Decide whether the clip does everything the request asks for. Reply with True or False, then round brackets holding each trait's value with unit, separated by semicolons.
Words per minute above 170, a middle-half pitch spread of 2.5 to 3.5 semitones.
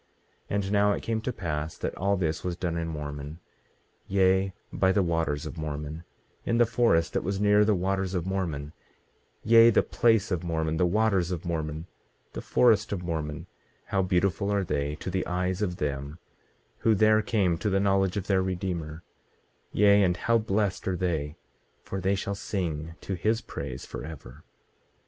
False (180 wpm; 3.9 semitones)